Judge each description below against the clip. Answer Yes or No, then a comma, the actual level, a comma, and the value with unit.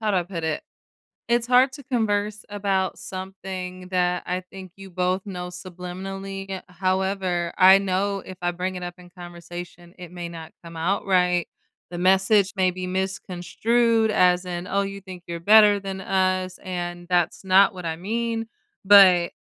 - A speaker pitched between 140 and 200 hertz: Yes, medium, 185 Hz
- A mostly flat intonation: Yes, narrow, 1.8 semitones